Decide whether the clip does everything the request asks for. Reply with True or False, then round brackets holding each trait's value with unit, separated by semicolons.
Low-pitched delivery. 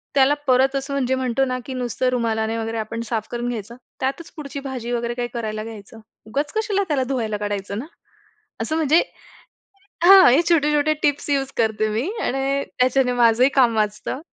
False (255 Hz)